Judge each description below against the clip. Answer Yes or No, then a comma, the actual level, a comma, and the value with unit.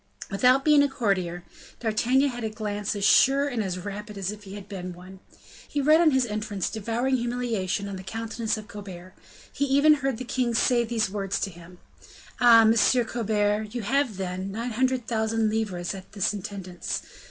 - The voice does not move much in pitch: No, average, 3.7 semitones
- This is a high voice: Yes, high, 215 Hz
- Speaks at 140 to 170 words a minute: No, average, 185 wpm